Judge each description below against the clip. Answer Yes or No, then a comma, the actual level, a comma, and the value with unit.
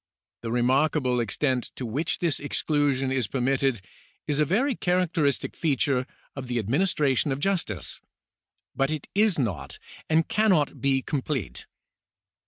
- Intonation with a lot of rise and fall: No, average, 3.7 semitones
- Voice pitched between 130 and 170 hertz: Yes, medium, 140 Hz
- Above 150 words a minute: No, slow, 135 wpm